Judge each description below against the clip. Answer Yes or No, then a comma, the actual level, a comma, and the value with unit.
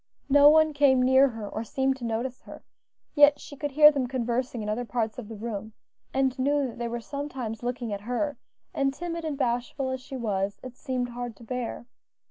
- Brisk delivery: Yes, fast, 210 wpm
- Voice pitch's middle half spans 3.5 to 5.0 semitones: No, average, 3.0 semitones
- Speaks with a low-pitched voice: No, very high, 255 Hz